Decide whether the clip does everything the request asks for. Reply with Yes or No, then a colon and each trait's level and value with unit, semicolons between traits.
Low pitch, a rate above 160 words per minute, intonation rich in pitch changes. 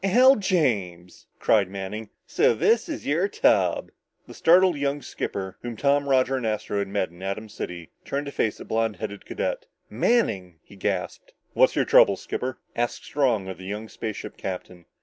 Yes: low, 110 Hz; average, 175 wpm; wide, 6.7 semitones